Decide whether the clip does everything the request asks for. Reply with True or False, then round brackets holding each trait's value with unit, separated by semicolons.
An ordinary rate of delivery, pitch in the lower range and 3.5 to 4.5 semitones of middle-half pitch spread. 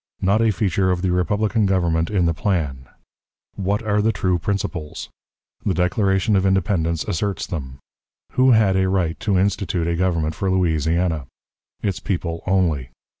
False (155 wpm; 95 Hz; 3.1 semitones)